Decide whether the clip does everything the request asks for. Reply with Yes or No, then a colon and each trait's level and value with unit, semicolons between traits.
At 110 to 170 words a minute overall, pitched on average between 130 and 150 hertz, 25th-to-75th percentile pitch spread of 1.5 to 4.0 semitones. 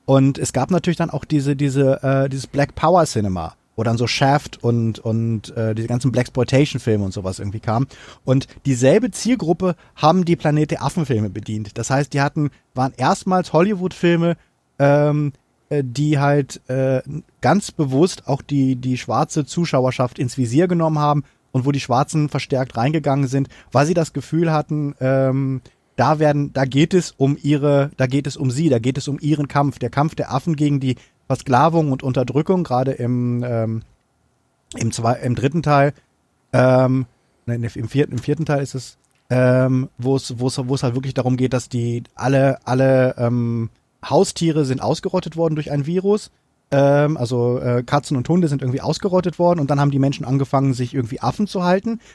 No: average, 180 wpm; low, 135 Hz; average, 3.0 semitones